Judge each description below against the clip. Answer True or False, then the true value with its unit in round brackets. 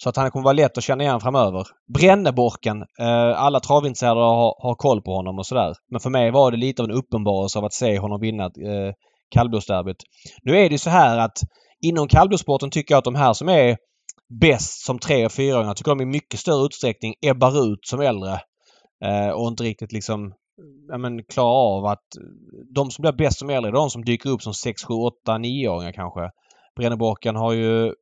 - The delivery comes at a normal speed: False (210 wpm)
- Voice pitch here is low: True (120 Hz)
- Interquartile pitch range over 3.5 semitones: True (4.2 semitones)